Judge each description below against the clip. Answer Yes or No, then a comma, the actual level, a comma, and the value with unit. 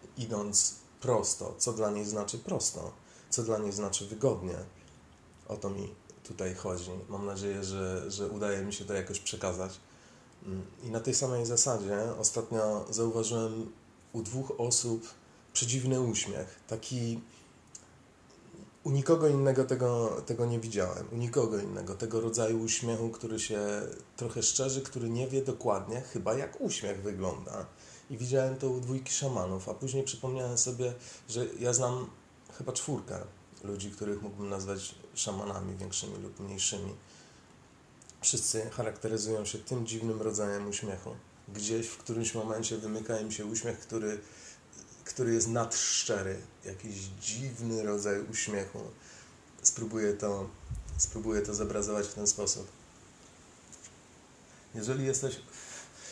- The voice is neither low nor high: No, low, 110 Hz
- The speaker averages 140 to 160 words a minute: No, average, 130 wpm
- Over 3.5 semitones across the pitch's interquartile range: No, average, 2.7 semitones